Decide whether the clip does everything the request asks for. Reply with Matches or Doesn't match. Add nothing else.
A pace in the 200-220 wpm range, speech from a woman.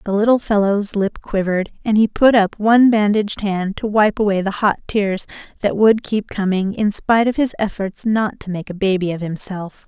Matches